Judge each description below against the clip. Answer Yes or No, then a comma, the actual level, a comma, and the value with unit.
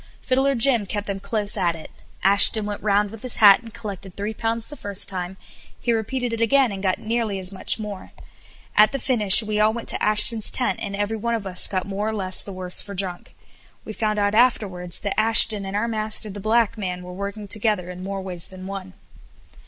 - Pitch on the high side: Yes, high, 205 Hz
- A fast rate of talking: Yes, fast, 220 wpm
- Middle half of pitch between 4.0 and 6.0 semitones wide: No, narrow, 2.5 semitones